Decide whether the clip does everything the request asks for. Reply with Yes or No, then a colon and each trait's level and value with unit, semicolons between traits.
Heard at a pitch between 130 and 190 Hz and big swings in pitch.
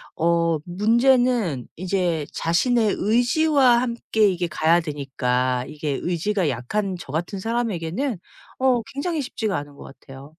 Yes: medium, 185 Hz; wide, 7.4 semitones